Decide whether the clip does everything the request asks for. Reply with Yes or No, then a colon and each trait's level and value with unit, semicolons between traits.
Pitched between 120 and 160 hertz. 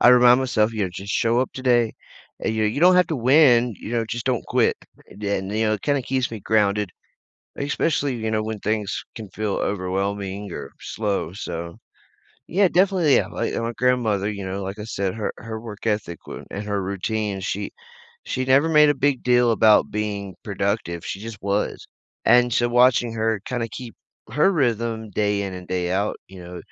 No: low, 110 Hz